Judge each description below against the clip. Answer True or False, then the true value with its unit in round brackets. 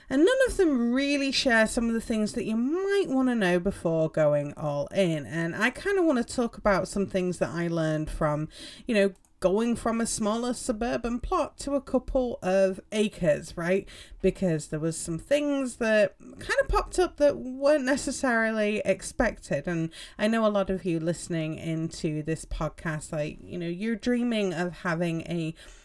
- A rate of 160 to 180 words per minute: False (190 wpm)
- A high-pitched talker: True (205 Hz)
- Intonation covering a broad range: True (7.1 semitones)